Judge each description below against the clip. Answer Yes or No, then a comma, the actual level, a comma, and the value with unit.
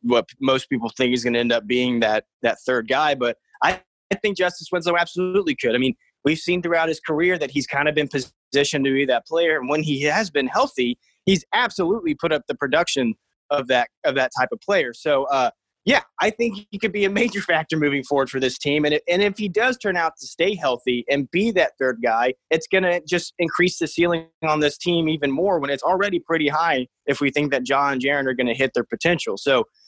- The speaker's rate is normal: No, fast, 235 wpm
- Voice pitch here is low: No, medium, 150 Hz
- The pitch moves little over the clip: No, average, 5.0 semitones